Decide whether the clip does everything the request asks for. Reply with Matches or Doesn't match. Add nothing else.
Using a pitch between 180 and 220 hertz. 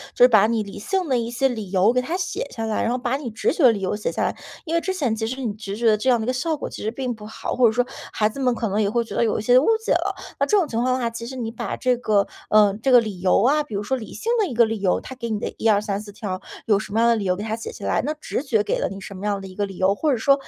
Doesn't match